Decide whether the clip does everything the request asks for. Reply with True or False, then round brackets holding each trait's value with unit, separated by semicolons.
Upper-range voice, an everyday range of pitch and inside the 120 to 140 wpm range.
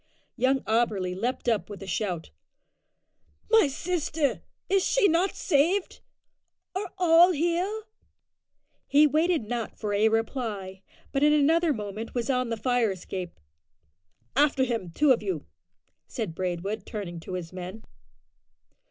False (245 Hz; 7.6 semitones; 135 wpm)